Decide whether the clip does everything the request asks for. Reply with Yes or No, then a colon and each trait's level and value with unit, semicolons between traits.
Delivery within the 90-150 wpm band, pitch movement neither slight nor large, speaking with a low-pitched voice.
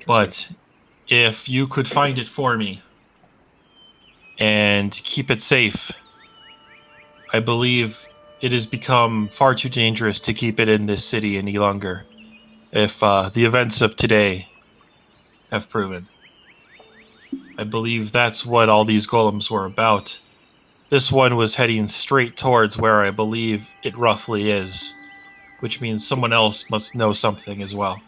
Yes: average, 140 wpm; average, 3.6 semitones; low, 115 Hz